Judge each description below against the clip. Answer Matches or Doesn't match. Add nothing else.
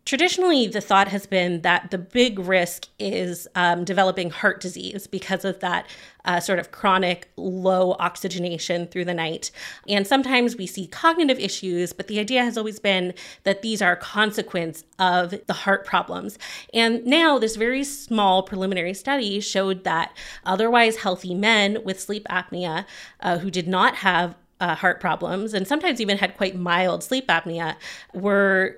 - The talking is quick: Doesn't match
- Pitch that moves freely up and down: Doesn't match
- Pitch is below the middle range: Doesn't match